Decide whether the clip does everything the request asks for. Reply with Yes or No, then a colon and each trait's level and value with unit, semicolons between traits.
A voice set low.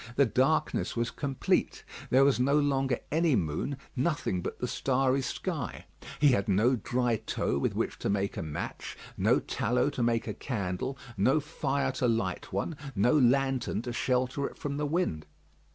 Yes: low, 130 Hz